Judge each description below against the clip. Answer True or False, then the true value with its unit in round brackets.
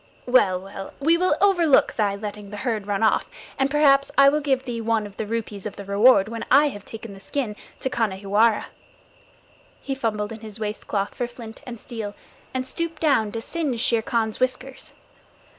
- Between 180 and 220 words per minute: True (190 wpm)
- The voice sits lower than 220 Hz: False (230 Hz)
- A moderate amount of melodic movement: True (4.3 semitones)